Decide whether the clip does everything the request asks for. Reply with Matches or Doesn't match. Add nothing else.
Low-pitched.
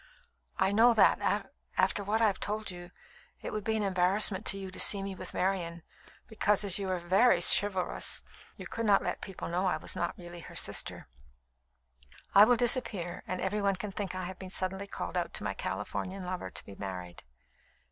Doesn't match